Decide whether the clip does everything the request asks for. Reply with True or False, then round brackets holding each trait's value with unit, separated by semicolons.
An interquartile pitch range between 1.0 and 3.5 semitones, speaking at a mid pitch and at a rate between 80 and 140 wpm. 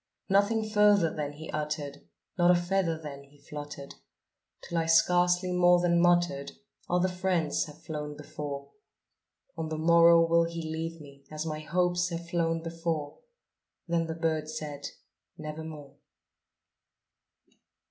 True (2.5 semitones; 165 Hz; 135 wpm)